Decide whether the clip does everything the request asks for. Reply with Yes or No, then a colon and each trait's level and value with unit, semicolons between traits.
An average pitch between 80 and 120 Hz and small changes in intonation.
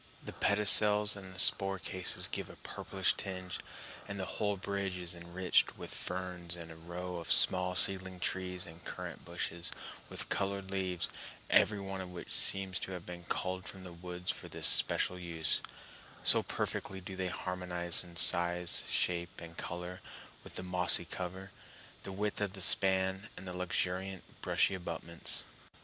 Yes: very low, 90 Hz; narrow, 1.5 semitones